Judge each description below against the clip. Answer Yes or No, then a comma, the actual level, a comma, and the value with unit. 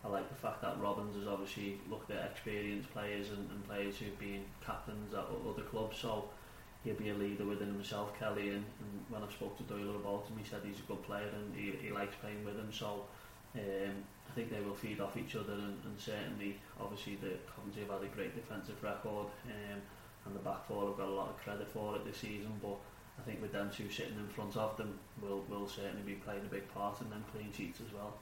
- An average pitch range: No, narrow, 1.0 semitones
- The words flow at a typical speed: No, fast, 240 wpm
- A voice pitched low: Yes, low, 105 Hz